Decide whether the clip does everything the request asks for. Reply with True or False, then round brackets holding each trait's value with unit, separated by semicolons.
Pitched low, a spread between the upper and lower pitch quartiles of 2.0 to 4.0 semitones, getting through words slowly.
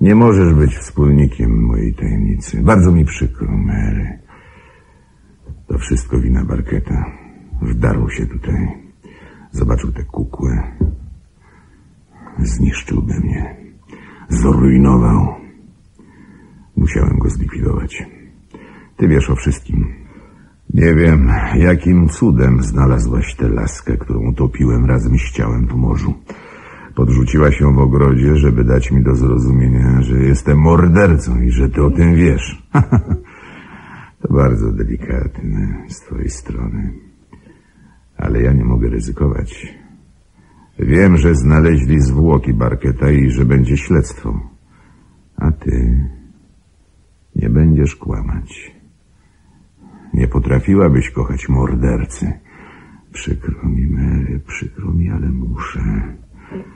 False (70 Hz; 4.4 semitones; 105 wpm)